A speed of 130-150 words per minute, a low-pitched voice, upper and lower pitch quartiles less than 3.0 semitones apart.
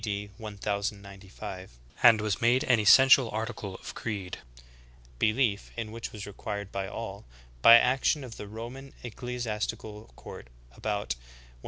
Yes: slow, 135 wpm; low, 105 Hz; narrow, 2.5 semitones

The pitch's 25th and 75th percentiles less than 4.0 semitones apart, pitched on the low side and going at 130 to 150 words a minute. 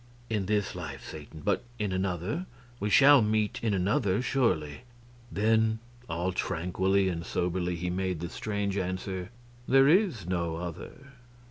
Yes: average, 3.5 semitones; very low, 95 Hz; average, 140 wpm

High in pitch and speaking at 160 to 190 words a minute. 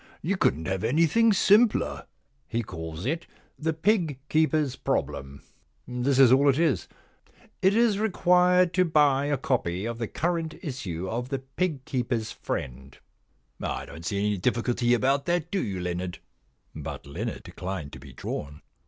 No: low, 130 Hz; average, 170 wpm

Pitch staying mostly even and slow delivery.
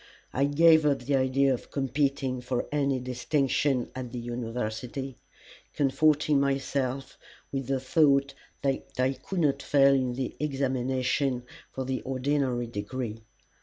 Yes: narrow, 1.7 semitones; slow, 130 wpm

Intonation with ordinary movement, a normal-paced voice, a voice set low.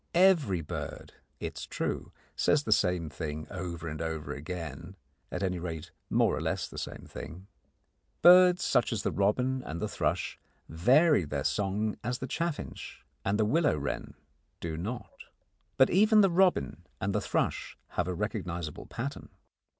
No: wide, 7.9 semitones; average, 160 wpm; low, 100 Hz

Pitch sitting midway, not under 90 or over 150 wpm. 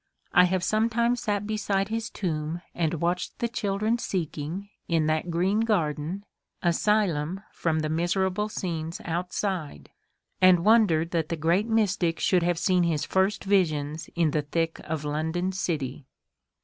Yes: medium, 175 Hz; average, 145 wpm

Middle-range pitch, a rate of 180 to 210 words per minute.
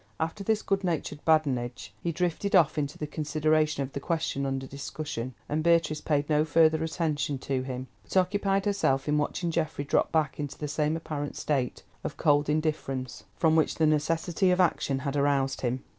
Yes: medium, 150 Hz; average, 185 wpm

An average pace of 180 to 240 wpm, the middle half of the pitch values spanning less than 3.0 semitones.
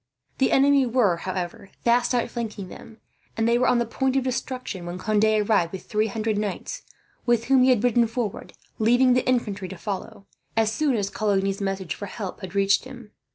No: average, 195 wpm; average, 3.8 semitones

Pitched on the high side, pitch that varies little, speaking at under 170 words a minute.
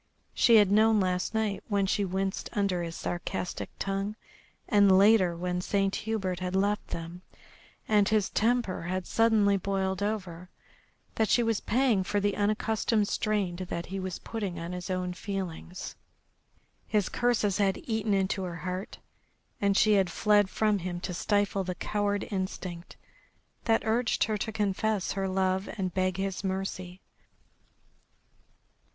Yes: high, 195 Hz; narrow, 2.3 semitones; average, 150 wpm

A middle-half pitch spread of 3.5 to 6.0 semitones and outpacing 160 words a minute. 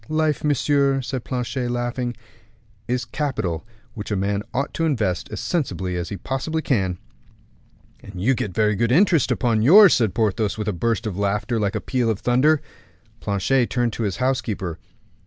Yes: average, 4.7 semitones; average, 175 wpm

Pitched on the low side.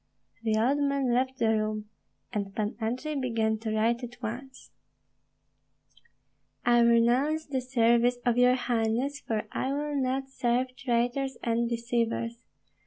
No: high, 240 Hz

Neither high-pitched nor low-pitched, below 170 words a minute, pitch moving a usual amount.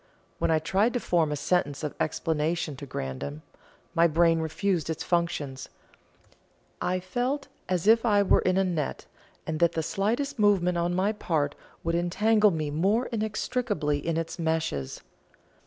Yes: medium, 170 Hz; average, 155 wpm; average, 4.5 semitones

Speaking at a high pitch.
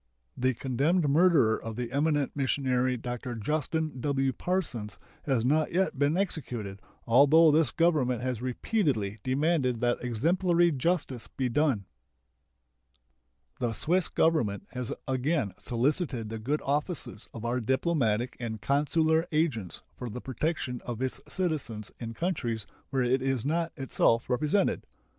No: low, 130 Hz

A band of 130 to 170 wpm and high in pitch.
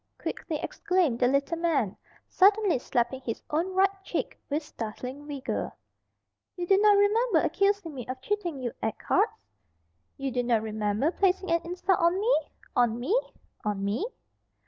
Yes: average, 155 wpm; very high, 310 Hz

